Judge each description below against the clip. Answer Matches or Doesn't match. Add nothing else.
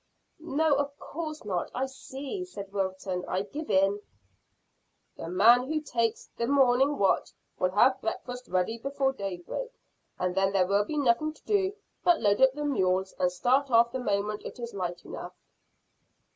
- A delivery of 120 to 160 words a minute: Doesn't match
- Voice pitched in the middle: Doesn't match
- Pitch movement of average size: Doesn't match